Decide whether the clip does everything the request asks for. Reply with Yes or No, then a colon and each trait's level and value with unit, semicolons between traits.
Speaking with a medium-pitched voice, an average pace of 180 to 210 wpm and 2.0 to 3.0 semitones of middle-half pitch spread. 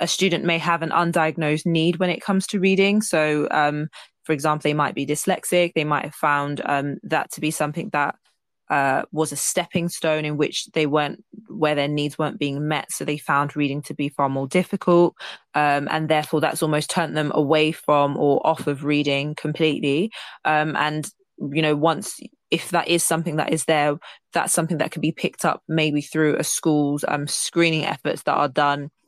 Yes: medium, 155 Hz; average, 200 wpm; narrow, 2.4 semitones